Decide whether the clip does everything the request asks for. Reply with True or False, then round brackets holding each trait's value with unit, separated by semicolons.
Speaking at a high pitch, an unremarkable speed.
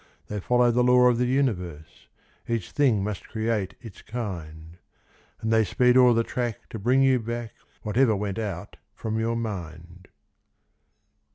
False (110 Hz; 155 wpm)